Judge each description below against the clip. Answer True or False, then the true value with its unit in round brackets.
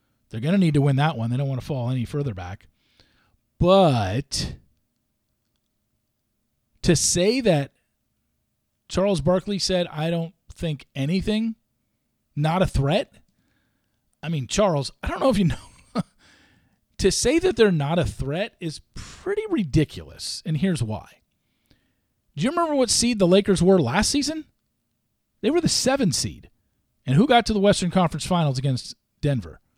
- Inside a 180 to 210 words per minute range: False (155 wpm)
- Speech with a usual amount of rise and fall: False (7.1 semitones)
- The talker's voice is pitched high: False (165 Hz)